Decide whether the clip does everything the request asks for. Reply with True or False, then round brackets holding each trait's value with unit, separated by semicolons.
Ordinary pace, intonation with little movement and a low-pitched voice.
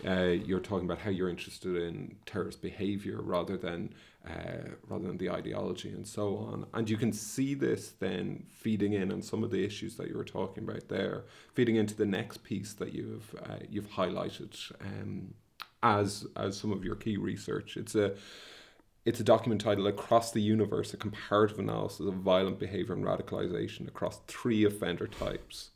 True (180 wpm; 2.3 semitones; 100 Hz)